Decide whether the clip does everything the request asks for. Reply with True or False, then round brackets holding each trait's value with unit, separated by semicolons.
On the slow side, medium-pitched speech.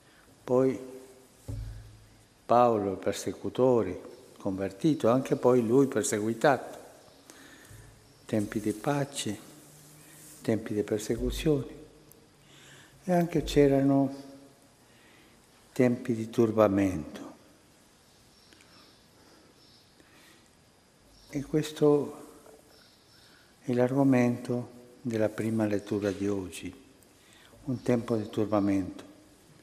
False (70 wpm; 125 Hz)